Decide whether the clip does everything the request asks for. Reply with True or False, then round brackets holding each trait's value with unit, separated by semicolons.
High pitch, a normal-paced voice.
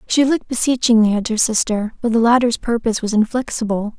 True (230 Hz; 180 wpm)